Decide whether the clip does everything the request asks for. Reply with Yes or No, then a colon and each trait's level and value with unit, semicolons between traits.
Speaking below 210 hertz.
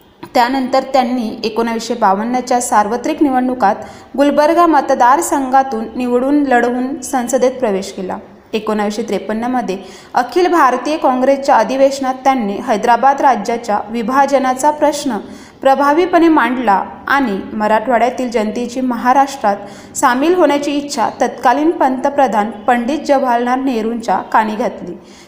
No: very high, 255 Hz